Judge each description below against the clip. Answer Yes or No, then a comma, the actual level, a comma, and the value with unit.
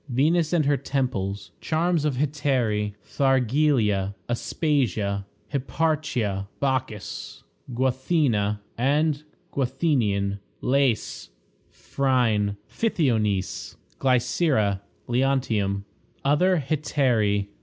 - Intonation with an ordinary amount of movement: No, wide, 5.7 semitones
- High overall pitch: No, low, 130 Hz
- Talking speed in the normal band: No, slow, 70 wpm